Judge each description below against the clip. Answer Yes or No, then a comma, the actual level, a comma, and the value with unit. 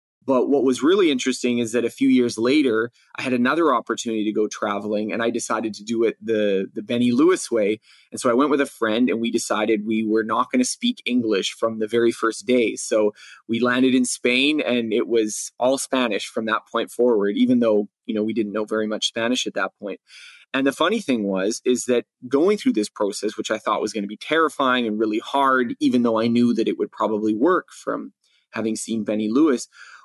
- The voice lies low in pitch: Yes, low, 115 Hz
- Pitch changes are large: No, average, 3.0 semitones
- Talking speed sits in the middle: No, fast, 230 wpm